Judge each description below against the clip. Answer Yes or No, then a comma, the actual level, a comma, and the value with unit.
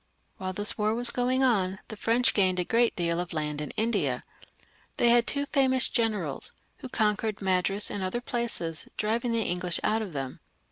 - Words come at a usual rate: Yes, average, 185 wpm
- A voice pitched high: Yes, high, 210 Hz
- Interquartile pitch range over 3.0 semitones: Yes, average, 4.5 semitones